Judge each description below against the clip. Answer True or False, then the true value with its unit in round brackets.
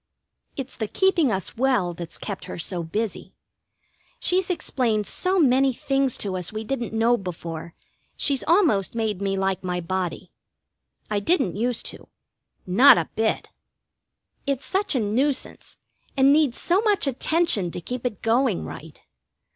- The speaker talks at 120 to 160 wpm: True (150 wpm)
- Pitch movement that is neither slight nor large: False (6.1 semitones)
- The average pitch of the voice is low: False (230 Hz)